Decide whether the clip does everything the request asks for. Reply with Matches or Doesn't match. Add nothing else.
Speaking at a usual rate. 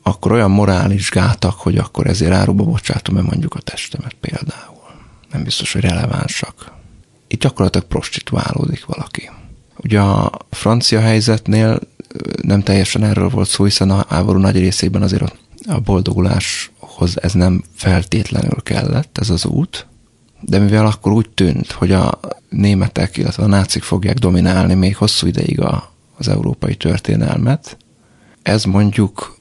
Matches